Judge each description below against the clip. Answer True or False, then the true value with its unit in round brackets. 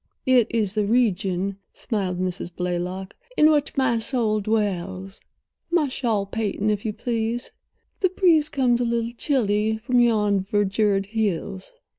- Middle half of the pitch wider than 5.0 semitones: False (3.6 semitones)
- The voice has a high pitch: True (215 Hz)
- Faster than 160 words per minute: False (135 wpm)